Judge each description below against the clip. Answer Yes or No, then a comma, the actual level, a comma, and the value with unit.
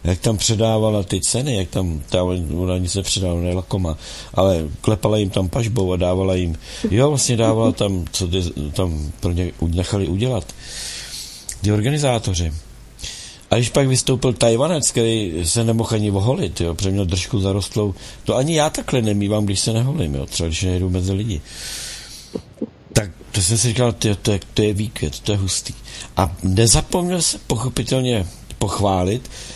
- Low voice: Yes, low, 100 Hz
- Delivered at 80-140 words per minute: No, average, 155 wpm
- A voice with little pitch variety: No, average, 4.1 semitones